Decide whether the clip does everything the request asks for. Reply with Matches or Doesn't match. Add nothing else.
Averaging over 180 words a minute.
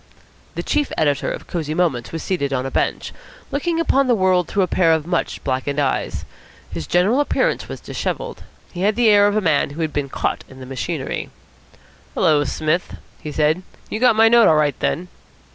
Matches